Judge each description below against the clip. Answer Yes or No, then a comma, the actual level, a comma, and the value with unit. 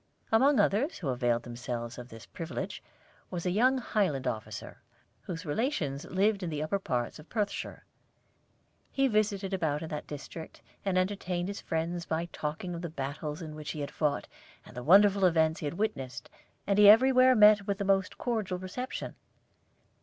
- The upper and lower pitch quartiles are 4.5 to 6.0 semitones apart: Yes, wide, 5.5 semitones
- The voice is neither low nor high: Yes, medium, 175 Hz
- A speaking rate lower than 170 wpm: No, average, 175 wpm